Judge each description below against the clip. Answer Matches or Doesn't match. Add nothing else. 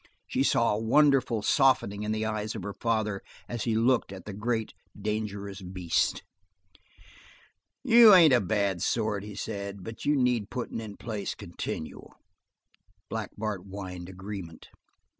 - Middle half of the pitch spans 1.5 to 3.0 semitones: Matches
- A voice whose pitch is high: Doesn't match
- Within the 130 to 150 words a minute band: Matches